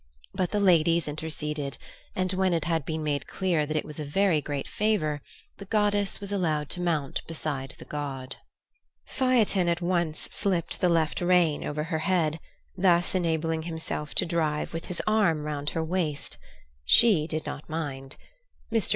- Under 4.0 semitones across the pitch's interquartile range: Yes, average, 3.4 semitones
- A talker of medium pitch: Yes, medium, 165 Hz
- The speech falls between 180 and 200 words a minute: No, average, 170 wpm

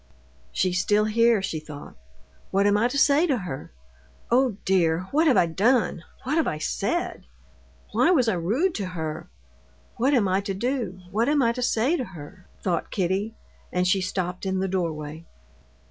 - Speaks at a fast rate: No, average, 180 wpm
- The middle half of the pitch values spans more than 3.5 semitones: Yes, wide, 5.4 semitones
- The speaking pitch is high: Yes, high, 195 Hz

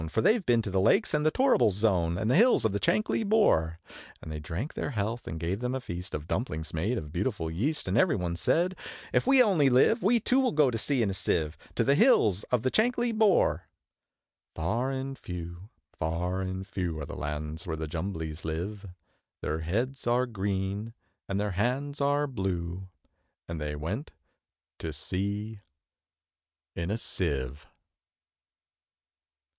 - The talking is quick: No, average, 175 wpm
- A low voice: Yes, low, 100 Hz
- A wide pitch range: Yes, wide, 8.0 semitones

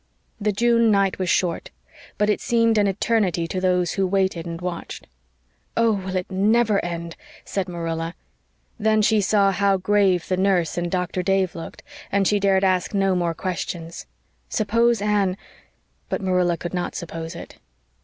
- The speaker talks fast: No, average, 165 wpm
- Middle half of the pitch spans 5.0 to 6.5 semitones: No, average, 2.7 semitones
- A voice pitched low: No, high, 190 Hz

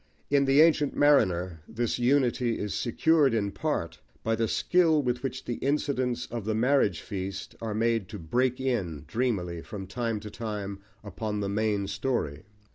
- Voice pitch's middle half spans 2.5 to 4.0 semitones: No, average, 4.5 semitones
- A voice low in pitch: Yes, low, 115 Hz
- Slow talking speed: No, average, 165 wpm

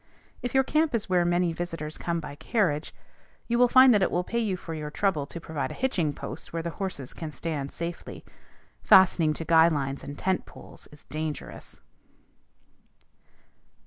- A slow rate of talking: No, average, 180 wpm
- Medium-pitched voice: Yes, medium, 170 Hz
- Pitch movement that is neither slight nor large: Yes, average, 4.1 semitones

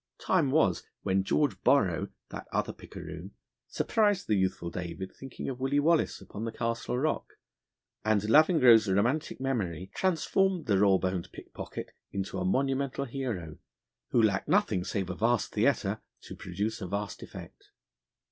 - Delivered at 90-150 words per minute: Yes, average, 145 wpm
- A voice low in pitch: Yes, low, 110 Hz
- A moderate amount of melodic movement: No, wide, 6.3 semitones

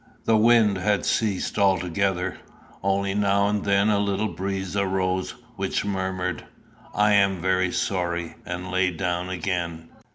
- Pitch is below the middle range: Yes, very low, 95 Hz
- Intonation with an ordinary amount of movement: No, narrow, 1.8 semitones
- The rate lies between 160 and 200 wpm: No, slow, 135 wpm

